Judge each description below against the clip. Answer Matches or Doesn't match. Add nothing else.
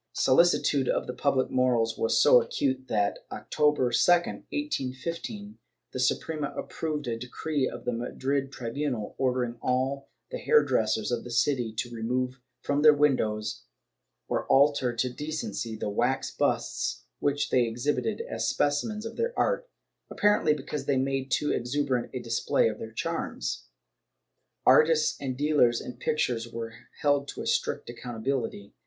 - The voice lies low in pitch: Matches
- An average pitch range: Matches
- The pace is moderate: Matches